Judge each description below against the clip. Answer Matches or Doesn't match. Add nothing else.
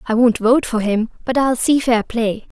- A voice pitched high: Matches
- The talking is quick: Matches